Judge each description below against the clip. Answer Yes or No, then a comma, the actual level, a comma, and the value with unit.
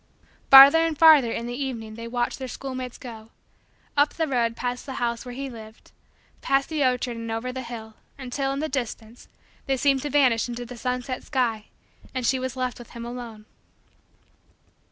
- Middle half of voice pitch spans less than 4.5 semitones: Yes, narrow, 2.5 semitones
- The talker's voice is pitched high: Yes, very high, 250 Hz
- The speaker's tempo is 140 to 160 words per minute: No, average, 185 wpm